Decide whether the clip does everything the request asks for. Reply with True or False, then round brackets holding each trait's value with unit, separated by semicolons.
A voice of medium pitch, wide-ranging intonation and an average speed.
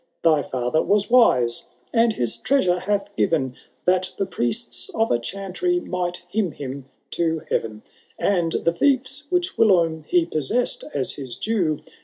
True (175 Hz; 6.6 semitones; 150 wpm)